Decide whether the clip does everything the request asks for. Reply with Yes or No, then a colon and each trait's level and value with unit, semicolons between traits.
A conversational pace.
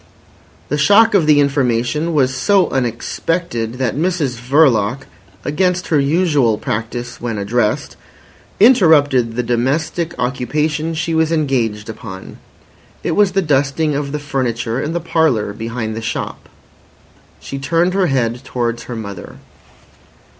No: slow, 130 wpm